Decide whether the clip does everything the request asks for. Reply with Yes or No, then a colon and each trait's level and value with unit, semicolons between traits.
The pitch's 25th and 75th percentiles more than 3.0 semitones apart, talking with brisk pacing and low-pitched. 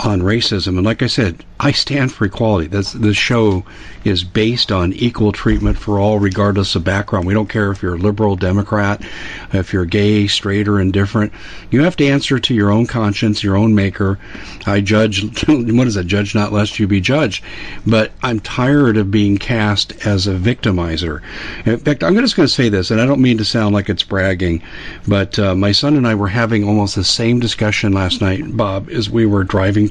No: narrow, 2.5 semitones; fast, 210 wpm; low, 105 Hz